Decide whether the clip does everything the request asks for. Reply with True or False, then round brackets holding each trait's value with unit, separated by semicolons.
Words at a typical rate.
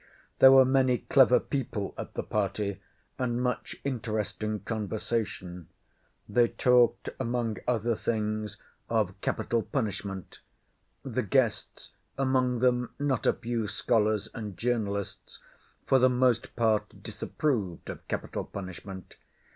False (115 wpm)